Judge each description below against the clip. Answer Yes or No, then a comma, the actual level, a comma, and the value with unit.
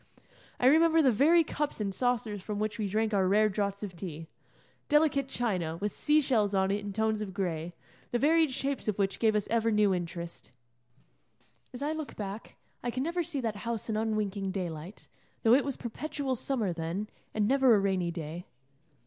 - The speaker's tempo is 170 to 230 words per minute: Yes, average, 190 wpm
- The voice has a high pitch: Yes, high, 215 Hz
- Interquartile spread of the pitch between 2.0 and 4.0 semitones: No, average, 5.1 semitones